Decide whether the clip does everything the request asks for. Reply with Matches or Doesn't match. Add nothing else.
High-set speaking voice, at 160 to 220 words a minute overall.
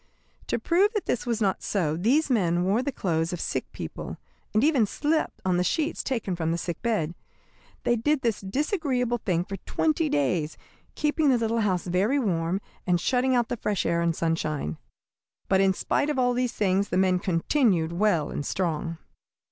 Matches